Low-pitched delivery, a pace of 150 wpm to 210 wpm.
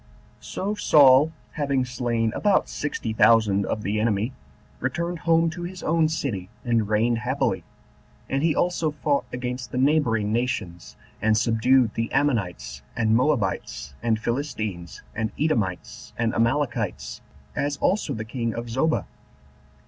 No: low, 120 Hz; average, 140 wpm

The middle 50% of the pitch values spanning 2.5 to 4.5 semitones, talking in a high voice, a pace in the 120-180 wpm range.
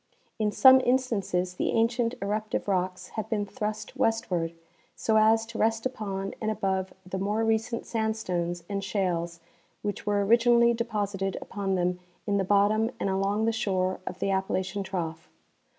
Yes: average, 2.8 semitones; high, 205 Hz; average, 155 wpm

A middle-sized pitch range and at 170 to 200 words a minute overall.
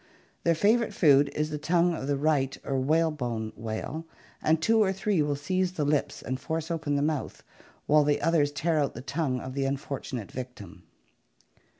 Yes: average, 3.2 semitones; average, 185 wpm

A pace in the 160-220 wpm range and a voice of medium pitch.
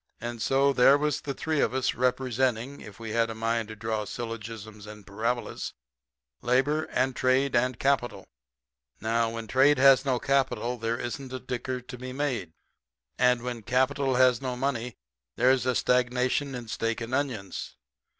No: average, 165 wpm; low, 125 Hz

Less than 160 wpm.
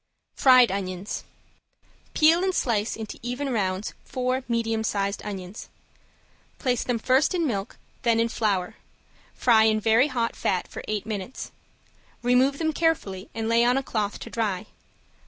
Yes: average, 150 wpm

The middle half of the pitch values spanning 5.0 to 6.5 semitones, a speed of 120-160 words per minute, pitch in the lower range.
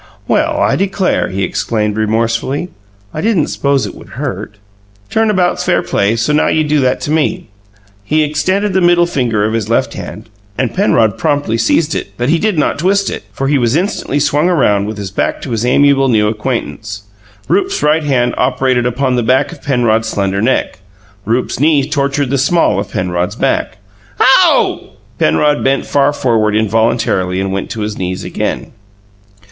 No: wide, 5.5 semitones; average, 175 wpm; low, 130 Hz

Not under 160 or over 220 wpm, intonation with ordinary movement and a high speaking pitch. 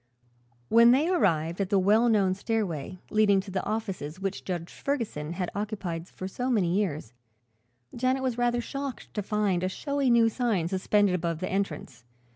Yes: average, 170 wpm; average, 4.4 semitones; high, 200 Hz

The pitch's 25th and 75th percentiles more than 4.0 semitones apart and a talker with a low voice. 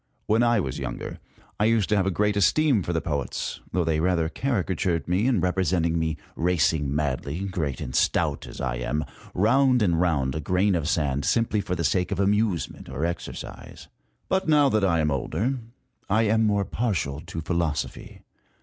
Yes: average, 5.1 semitones; very low, 90 Hz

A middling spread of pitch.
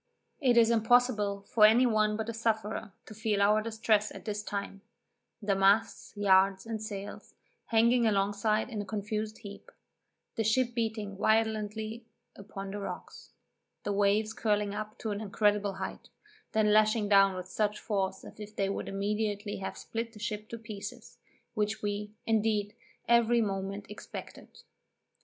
No: narrow, 1.6 semitones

